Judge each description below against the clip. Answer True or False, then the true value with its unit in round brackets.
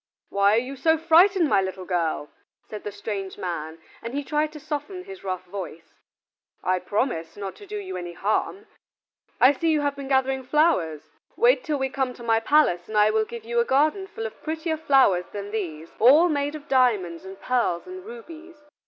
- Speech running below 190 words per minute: False (200 wpm)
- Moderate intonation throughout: False (8.0 semitones)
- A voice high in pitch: True (255 Hz)